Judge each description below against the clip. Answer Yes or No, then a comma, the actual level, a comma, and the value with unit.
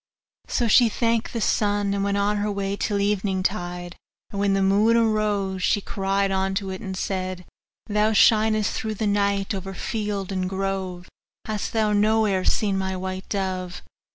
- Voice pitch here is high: Yes, high, 200 Hz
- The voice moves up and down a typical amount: No, narrow, 1.7 semitones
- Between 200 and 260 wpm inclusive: No, average, 165 wpm